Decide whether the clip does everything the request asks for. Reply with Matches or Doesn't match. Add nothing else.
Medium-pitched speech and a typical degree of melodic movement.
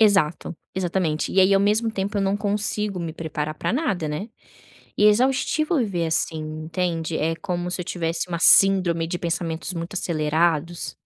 Matches